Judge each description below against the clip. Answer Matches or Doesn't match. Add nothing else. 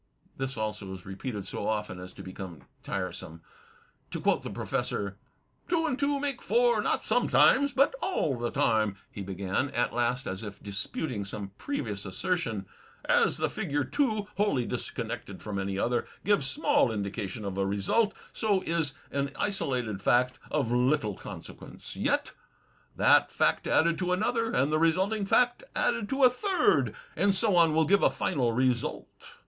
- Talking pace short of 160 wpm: Doesn't match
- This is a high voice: Doesn't match